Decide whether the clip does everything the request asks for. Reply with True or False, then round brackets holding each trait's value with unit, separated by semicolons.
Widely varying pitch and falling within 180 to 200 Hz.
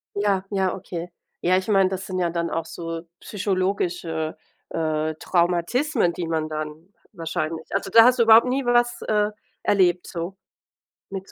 False (3.5 semitones; 185 Hz)